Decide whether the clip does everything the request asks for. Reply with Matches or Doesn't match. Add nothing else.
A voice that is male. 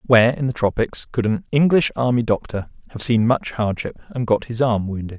Matches